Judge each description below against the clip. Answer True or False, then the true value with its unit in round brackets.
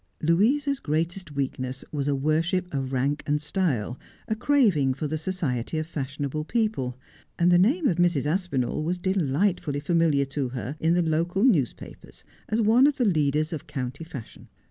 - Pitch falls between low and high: True (155 Hz)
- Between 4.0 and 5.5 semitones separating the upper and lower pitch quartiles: True (4.8 semitones)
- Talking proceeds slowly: False (175 wpm)